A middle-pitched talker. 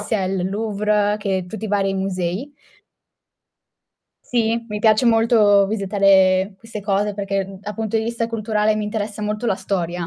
No: high, 210 Hz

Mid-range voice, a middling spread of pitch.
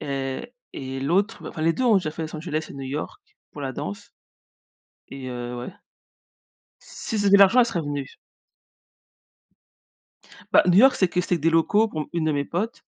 No: medium, 160 Hz; wide, 5.9 semitones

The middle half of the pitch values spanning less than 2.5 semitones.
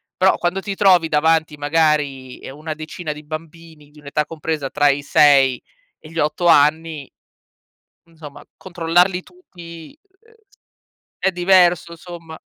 No: average, 2.8 semitones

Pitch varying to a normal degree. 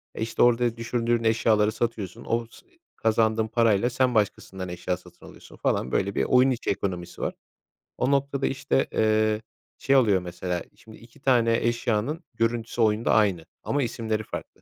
No: narrow, 2.2 semitones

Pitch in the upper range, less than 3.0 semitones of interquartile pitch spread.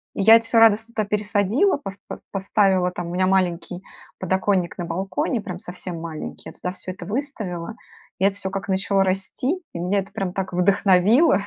Yes: high, 195 Hz; narrow, 2.6 semitones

